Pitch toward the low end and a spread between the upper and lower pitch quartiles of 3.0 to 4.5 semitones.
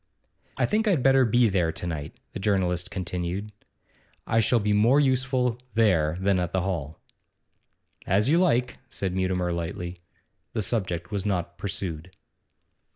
No: very low, 95 Hz; average, 5.0 semitones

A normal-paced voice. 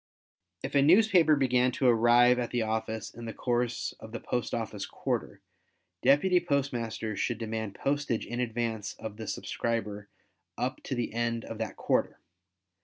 Yes: average, 160 wpm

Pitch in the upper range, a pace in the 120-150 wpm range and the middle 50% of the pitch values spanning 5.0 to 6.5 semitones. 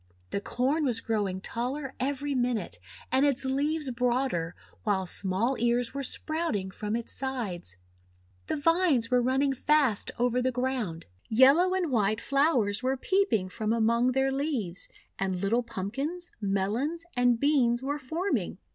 No: very high, 250 Hz; average, 145 wpm; average, 4.5 semitones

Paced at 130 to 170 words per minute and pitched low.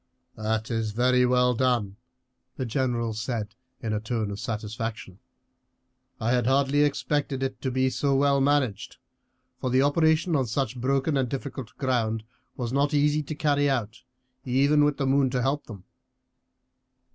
Yes: average, 155 wpm; low, 130 Hz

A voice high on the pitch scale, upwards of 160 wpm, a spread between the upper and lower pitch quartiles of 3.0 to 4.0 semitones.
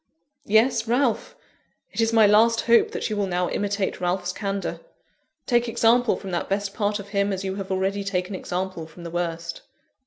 Yes: high, 200 Hz; average, 185 wpm; average, 3.3 semitones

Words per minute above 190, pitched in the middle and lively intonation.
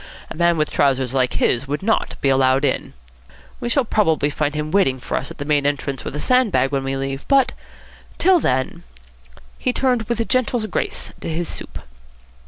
Yes: average, 200 wpm; medium, 150 Hz; wide, 8.3 semitones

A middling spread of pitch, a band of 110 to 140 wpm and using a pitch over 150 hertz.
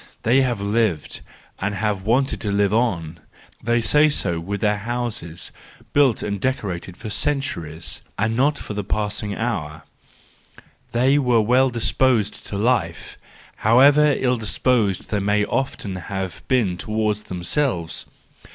No: average, 4.3 semitones; slow, 135 wpm; low, 110 Hz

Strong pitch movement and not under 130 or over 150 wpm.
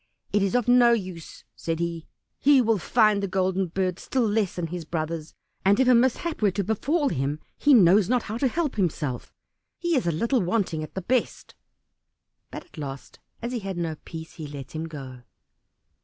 No: wide, 6.4 semitones; average, 200 wpm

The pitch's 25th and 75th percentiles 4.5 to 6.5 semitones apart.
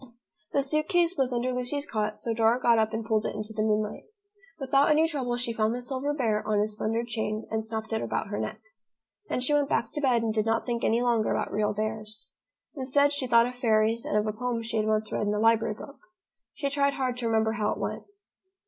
No: average, 3.0 semitones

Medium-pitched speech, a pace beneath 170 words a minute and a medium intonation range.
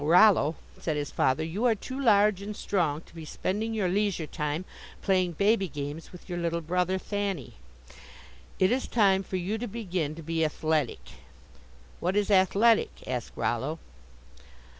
Yes: medium, 180 Hz; average, 160 wpm; average, 4.4 semitones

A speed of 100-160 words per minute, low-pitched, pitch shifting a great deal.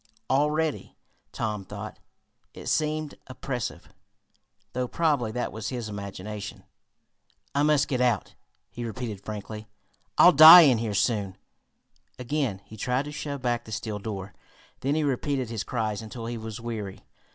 No: average, 145 wpm; low, 120 Hz; average, 4.5 semitones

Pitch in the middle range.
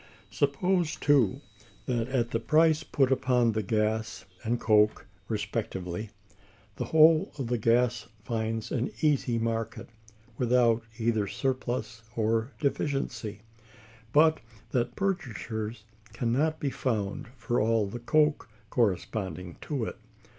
No: low, 120 Hz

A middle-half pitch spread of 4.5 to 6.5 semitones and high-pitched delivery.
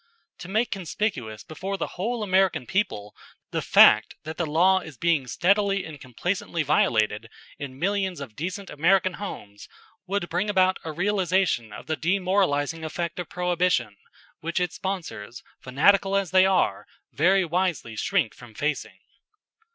No: average, 4.9 semitones; medium, 175 Hz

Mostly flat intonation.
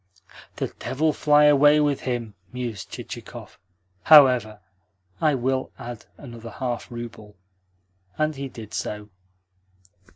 No: average, 4.2 semitones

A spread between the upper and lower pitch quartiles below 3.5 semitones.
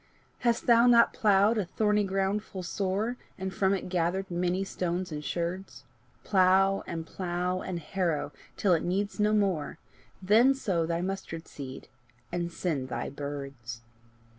Yes: average, 2.8 semitones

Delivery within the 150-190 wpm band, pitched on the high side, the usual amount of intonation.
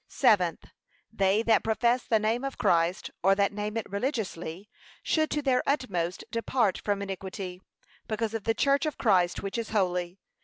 Yes: average, 165 wpm; high, 210 Hz; average, 3.7 semitones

